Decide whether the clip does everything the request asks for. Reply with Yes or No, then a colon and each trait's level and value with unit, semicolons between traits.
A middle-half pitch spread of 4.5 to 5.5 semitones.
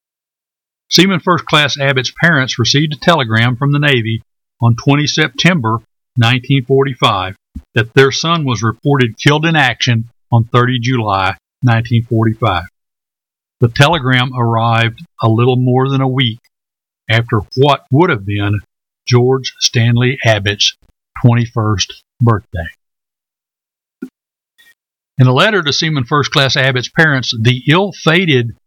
No: average, 3.6 semitones